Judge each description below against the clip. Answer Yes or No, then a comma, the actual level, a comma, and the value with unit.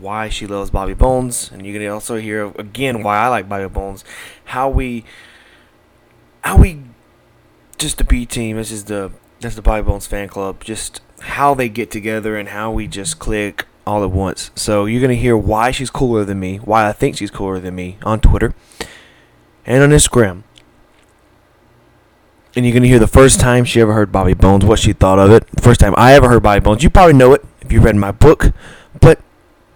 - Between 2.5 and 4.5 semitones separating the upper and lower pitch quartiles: Yes, average, 3.3 semitones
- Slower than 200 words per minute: No, fast, 205 wpm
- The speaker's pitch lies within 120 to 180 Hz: No, low, 105 Hz